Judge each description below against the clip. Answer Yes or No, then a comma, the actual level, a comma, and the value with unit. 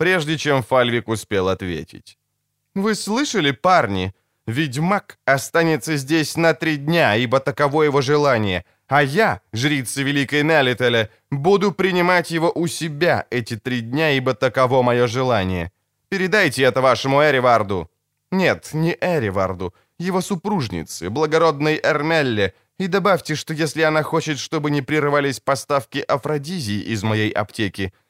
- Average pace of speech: Yes, average, 130 wpm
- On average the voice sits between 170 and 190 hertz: No, medium, 140 Hz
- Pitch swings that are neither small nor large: No, wide, 5.9 semitones